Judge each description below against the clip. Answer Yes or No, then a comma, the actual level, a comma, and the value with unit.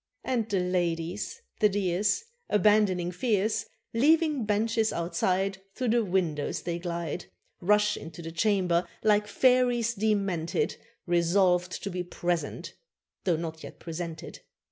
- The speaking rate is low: Yes, slow, 120 wpm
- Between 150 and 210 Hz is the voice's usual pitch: Yes, high, 190 Hz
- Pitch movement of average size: Yes, average, 3.8 semitones